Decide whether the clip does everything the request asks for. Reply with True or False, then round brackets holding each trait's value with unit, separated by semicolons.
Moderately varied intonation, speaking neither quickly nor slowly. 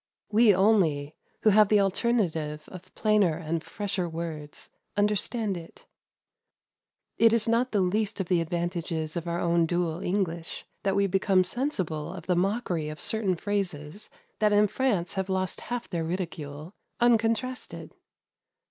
True (4.1 semitones; 145 wpm)